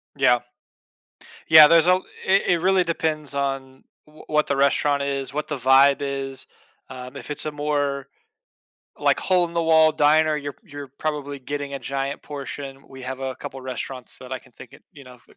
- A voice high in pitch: No, medium, 140 Hz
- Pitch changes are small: Yes, narrow, 2.1 semitones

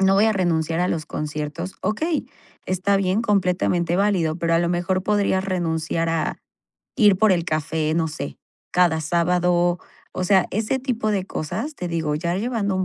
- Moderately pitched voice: Yes, medium, 180 Hz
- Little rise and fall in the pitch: No, average, 3.2 semitones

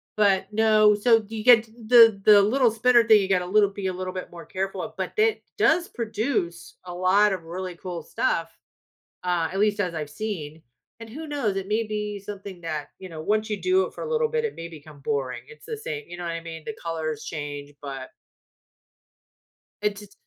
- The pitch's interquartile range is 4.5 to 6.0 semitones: Yes, average, 4.8 semitones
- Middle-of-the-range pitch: No, high, 200 Hz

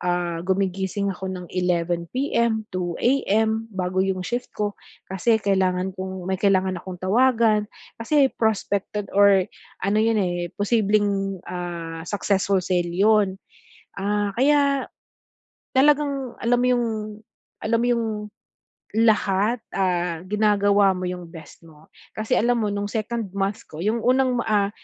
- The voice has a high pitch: Yes, high, 200 Hz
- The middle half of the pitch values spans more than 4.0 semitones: No, average, 3.4 semitones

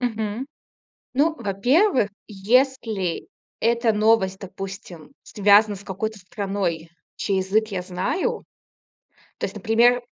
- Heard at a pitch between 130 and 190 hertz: No, high, 210 Hz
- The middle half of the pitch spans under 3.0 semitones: No, average, 3.4 semitones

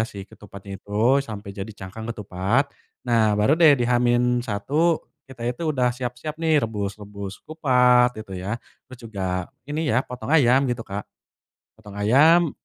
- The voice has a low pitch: Yes, low, 120 Hz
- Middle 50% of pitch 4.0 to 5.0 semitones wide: Yes, average, 4.5 semitones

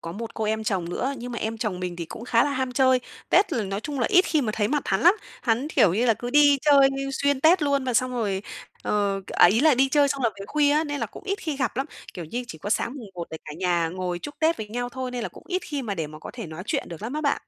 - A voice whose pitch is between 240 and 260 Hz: Yes, high, 245 Hz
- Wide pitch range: Yes, wide, 6.0 semitones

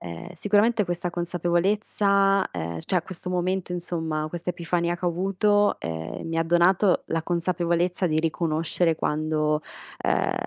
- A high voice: No, medium, 175 Hz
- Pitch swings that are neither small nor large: No, narrow, 2.3 semitones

